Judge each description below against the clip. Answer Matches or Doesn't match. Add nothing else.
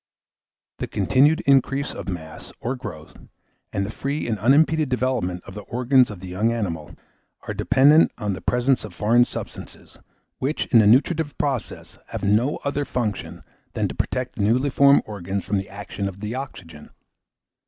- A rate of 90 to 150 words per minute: Doesn't match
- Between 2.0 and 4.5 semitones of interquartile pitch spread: Doesn't match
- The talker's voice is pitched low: Matches